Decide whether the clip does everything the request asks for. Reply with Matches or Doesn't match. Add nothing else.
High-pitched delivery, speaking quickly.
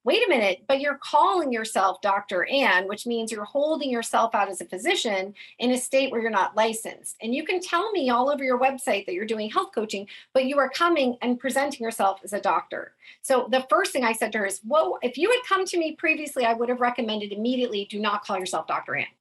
Matches